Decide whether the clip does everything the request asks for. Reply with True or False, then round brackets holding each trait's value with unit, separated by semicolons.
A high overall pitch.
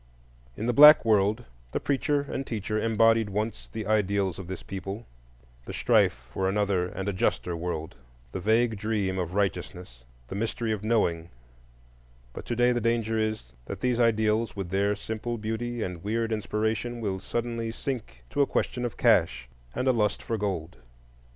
False (105 Hz)